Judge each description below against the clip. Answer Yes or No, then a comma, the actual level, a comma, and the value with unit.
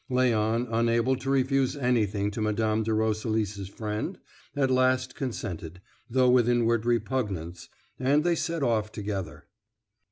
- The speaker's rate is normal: No, slow, 130 wpm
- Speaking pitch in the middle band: No, low, 115 Hz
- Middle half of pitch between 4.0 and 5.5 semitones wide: No, average, 3.4 semitones